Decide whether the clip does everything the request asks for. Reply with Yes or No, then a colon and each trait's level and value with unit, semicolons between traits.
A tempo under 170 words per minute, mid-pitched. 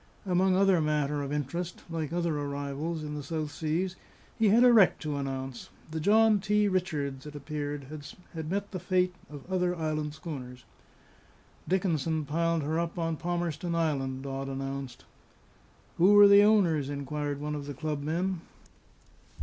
Yes: average, 160 wpm; medium, 155 Hz